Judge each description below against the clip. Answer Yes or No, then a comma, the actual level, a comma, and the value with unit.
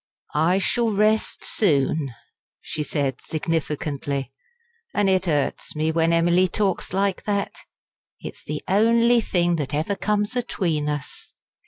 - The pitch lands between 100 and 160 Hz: No, medium, 175 Hz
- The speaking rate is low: Yes, slow, 130 wpm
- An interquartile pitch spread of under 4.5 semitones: No, average, 5.1 semitones